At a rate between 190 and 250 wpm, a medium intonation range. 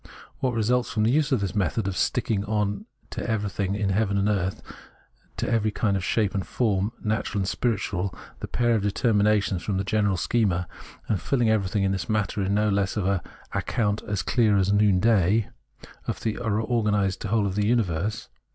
No: average, 195 wpm; narrow, 2.1 semitones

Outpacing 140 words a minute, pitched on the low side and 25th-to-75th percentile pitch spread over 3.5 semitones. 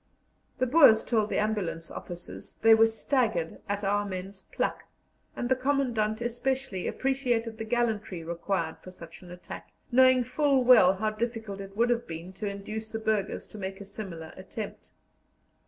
No: average, 165 wpm; high, 215 Hz; average, 3.9 semitones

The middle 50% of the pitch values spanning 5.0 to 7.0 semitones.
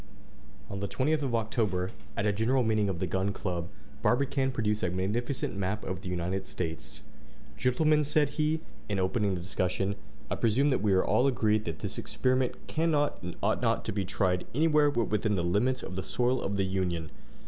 Yes: wide, 5.6 semitones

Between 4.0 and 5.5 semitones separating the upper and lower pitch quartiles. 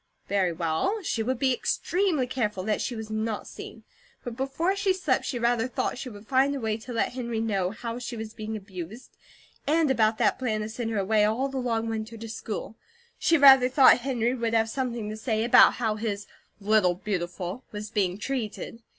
No: average, 3.3 semitones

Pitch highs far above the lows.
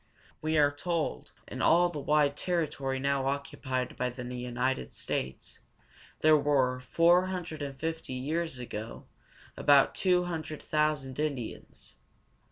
No: average, 3.5 semitones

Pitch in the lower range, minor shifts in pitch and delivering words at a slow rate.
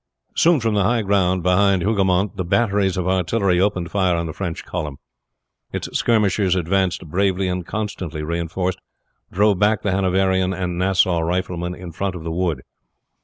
No: very low, 95 Hz; narrow, 2.0 semitones; average, 165 wpm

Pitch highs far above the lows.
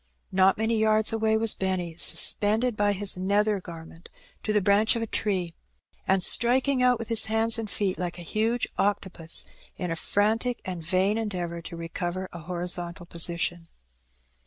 No: average, 3.9 semitones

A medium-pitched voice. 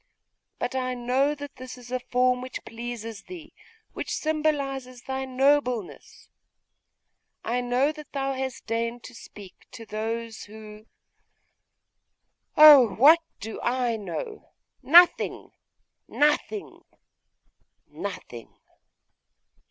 No: very high, 250 Hz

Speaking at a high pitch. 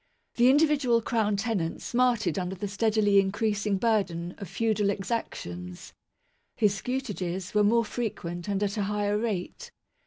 Yes: high, 205 Hz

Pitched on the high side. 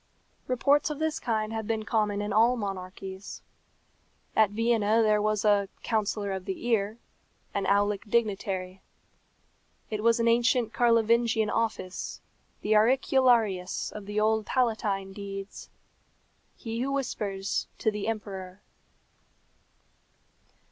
Yes: high, 215 Hz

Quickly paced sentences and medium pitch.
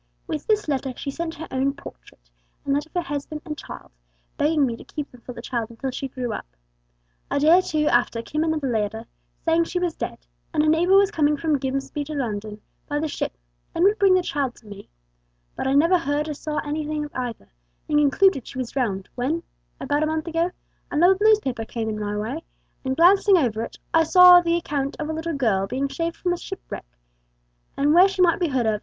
No: fast, 225 wpm; very high, 290 Hz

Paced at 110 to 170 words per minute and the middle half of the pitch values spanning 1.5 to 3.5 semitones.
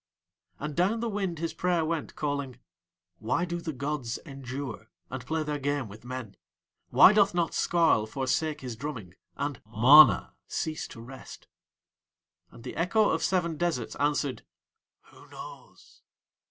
No: average, 145 wpm; average, 4.7 semitones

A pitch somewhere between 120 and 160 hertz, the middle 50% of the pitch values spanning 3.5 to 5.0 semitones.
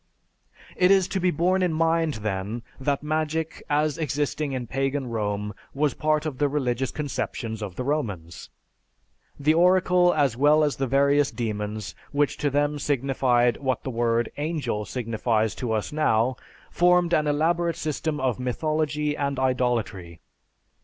Yes: medium, 140 Hz; average, 4.5 semitones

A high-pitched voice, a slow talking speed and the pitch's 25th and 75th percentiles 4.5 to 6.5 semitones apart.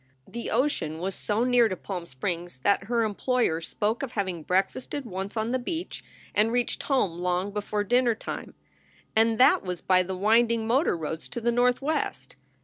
No: high, 215 Hz; average, 175 wpm; average, 4.8 semitones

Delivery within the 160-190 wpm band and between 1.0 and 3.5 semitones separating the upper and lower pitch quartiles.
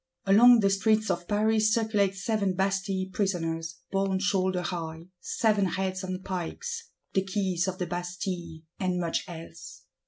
No: average, 145 wpm; narrow, 2.4 semitones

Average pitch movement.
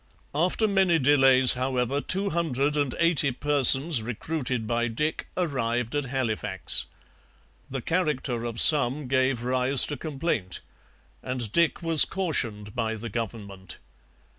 Yes: average, 4.3 semitones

